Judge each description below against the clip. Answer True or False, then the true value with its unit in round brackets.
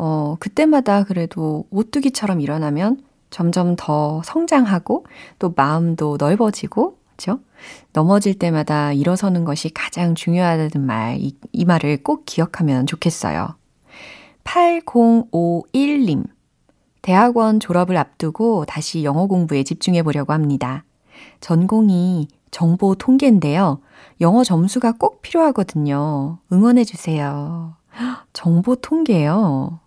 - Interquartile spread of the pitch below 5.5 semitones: False (6.7 semitones)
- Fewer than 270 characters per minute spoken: True (255 characters per minute)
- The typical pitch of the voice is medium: True (175 Hz)